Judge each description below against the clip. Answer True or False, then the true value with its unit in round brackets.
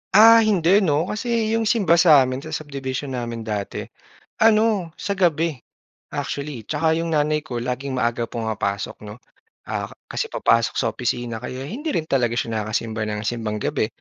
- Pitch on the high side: False (140 Hz)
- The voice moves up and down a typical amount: False (6.7 semitones)